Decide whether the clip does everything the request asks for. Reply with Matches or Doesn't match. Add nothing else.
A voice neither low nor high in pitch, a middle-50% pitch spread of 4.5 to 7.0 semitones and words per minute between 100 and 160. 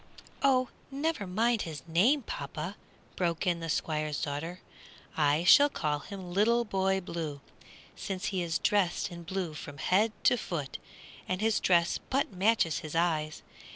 Matches